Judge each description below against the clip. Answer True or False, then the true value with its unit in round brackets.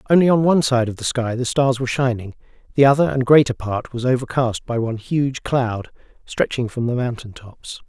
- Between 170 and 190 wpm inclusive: False (200 wpm)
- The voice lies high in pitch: False (125 Hz)